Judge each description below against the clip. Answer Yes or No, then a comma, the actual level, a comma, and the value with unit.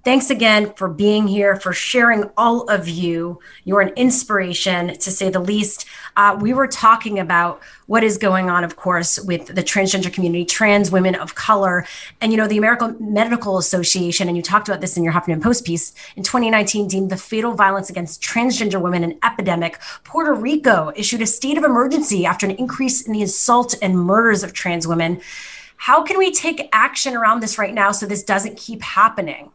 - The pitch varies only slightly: No, average, 4.0 semitones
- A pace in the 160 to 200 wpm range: Yes, average, 195 wpm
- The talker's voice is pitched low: No, high, 205 Hz